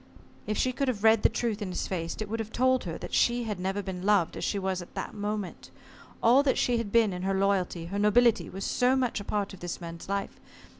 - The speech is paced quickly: Yes, fast, 255 wpm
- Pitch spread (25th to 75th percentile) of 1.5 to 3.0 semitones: No, average, 3.4 semitones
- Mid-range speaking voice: No, high, 205 Hz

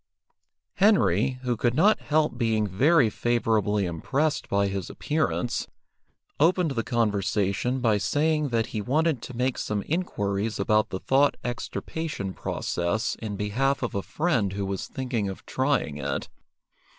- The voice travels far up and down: Yes, wide, 5.9 semitones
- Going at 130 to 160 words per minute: Yes, average, 140 wpm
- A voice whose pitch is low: Yes, low, 115 Hz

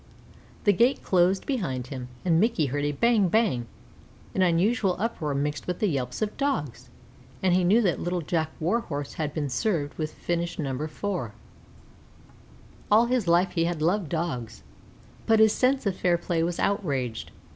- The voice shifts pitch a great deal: Yes, wide, 5.8 semitones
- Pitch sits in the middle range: Yes, medium, 175 Hz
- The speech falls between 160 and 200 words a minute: Yes, average, 165 wpm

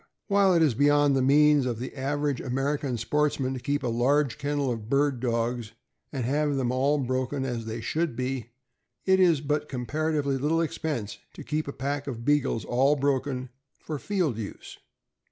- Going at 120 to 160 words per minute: No, average, 175 wpm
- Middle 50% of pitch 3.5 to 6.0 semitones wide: No, average, 2.9 semitones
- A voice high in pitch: No, medium, 140 Hz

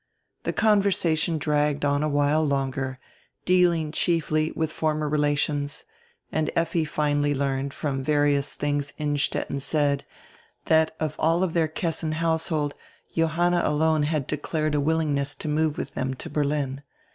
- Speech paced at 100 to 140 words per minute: Yes, slow, 135 wpm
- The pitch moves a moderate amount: No, narrow, 1.9 semitones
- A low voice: No, medium, 150 Hz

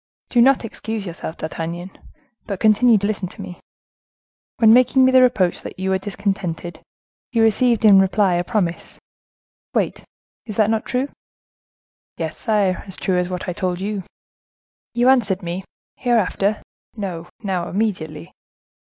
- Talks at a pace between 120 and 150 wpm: Yes, average, 145 wpm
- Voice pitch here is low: No, high, 200 Hz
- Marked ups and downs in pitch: No, average, 3.8 semitones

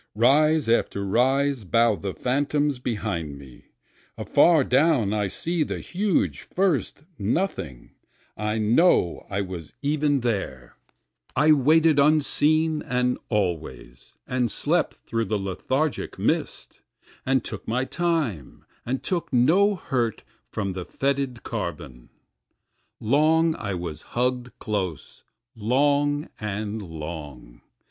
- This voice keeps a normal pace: No, slow, 115 wpm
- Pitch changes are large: Yes, wide, 6.9 semitones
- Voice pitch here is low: Yes, low, 125 Hz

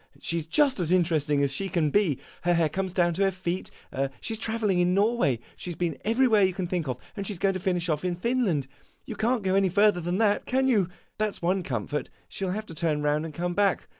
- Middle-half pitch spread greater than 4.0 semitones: No, average, 3.7 semitones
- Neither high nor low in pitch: Yes, medium, 180 Hz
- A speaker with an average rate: No, fast, 255 wpm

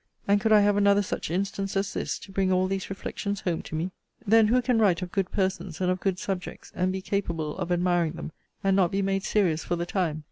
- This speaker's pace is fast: Yes, fast, 245 wpm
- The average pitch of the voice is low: No, high, 190 Hz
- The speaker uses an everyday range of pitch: No, narrow, 2.0 semitones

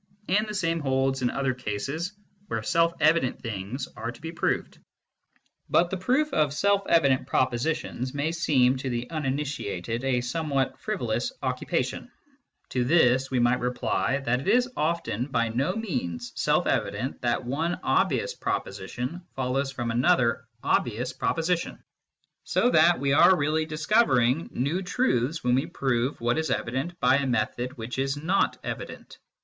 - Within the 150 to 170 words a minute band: Yes, average, 155 wpm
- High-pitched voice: No, low, 135 Hz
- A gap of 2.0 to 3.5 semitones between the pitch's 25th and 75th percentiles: No, average, 4.8 semitones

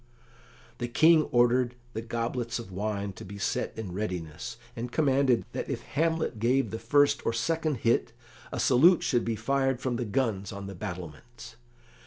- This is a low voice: Yes, low, 120 Hz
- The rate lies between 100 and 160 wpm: No, average, 170 wpm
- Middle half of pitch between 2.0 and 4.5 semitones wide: Yes, average, 4.0 semitones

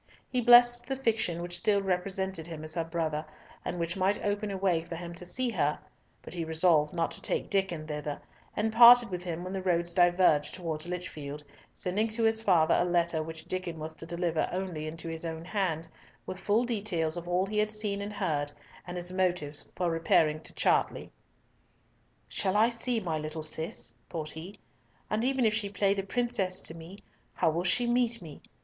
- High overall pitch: No, medium, 180 Hz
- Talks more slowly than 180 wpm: No, average, 200 wpm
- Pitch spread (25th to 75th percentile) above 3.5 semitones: Yes, average, 3.9 semitones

